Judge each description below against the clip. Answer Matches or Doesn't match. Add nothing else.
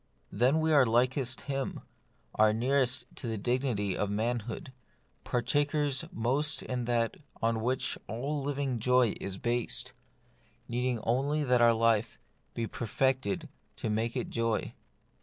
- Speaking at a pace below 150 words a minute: Matches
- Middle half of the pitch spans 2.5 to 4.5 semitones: Matches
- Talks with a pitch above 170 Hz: Doesn't match